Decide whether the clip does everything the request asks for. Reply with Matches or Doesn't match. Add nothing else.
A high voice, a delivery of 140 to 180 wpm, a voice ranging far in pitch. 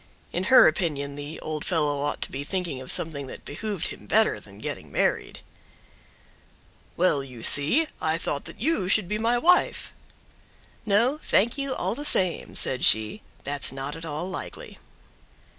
Doesn't match